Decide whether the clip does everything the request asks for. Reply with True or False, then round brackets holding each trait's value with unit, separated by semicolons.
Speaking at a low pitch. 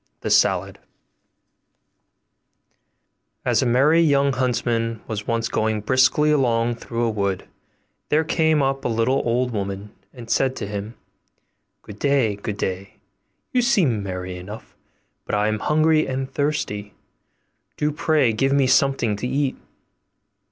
True (120 Hz)